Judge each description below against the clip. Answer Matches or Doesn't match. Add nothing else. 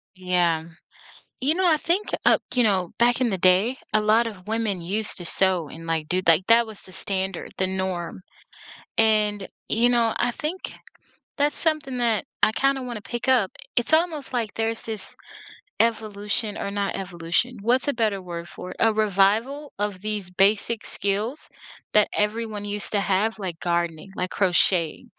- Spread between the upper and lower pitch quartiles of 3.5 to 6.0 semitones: Matches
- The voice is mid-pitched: Doesn't match